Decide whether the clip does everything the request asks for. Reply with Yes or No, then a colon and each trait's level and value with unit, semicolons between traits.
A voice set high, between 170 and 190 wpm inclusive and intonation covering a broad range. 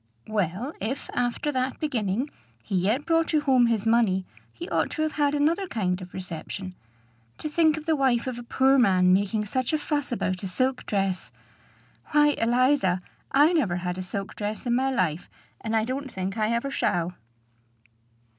Yes: high, 235 Hz; average, 185 wpm; wide, 6.5 semitones